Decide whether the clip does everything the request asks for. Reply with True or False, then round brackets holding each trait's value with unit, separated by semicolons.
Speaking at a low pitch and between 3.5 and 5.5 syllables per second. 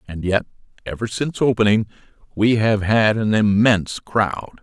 True (105 Hz; 4.7 syllables/s)